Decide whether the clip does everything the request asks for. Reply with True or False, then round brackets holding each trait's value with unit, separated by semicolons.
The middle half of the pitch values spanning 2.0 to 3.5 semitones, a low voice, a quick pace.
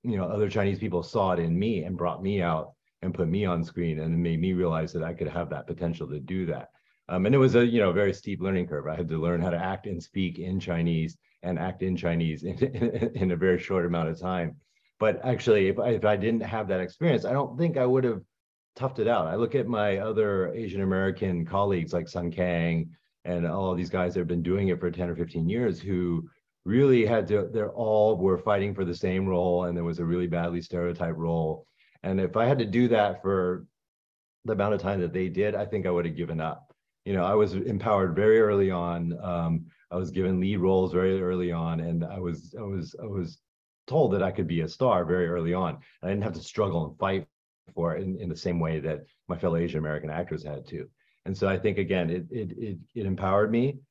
True (2.7 semitones; 90 Hz; 245 wpm)